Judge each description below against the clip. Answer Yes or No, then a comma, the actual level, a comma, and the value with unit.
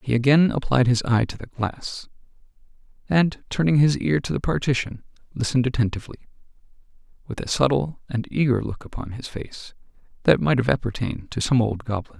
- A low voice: Yes, low, 125 Hz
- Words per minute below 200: Yes, average, 165 wpm